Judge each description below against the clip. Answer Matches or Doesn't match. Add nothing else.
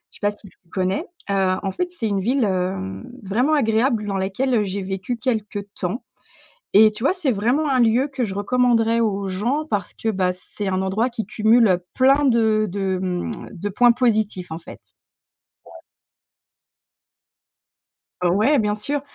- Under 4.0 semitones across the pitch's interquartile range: Doesn't match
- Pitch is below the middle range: Doesn't match